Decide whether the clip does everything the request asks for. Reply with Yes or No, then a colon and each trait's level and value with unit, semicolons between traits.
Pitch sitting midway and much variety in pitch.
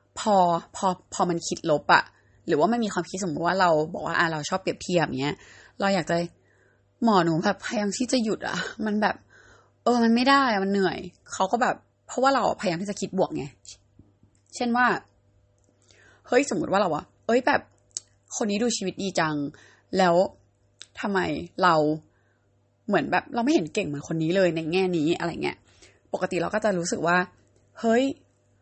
Yes: medium, 180 Hz; wide, 7.0 semitones